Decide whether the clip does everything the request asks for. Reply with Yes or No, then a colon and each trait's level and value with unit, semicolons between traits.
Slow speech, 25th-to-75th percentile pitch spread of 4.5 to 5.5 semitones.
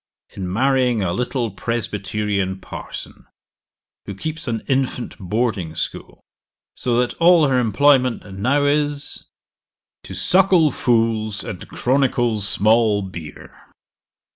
Yes: slow, 110 wpm; average, 4.9 semitones